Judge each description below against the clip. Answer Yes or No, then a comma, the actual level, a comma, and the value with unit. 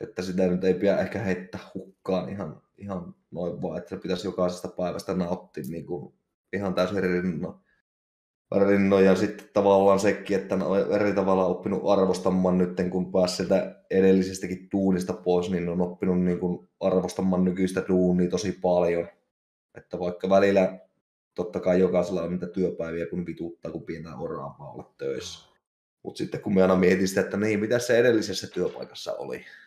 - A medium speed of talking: No, fast, 170 wpm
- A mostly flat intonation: Yes, narrow, 1.1 semitones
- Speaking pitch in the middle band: No, very low, 95 Hz